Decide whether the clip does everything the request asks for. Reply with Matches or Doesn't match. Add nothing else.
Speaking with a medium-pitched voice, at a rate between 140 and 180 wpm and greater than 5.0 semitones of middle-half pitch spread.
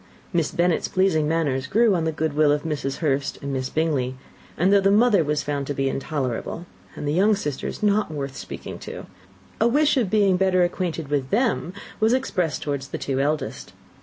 Doesn't match